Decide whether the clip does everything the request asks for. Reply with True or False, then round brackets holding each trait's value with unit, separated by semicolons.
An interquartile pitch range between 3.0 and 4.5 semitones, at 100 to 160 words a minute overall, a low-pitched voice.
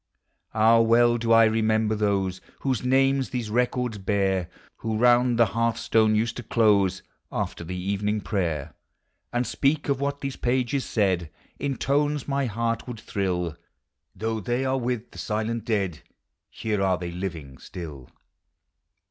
True (4.0 semitones; 150 wpm; 110 Hz)